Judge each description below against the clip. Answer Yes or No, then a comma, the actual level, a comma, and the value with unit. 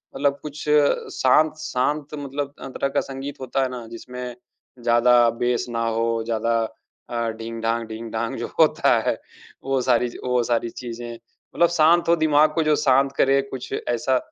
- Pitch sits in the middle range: No, low, 125 Hz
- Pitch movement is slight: No, average, 3.2 semitones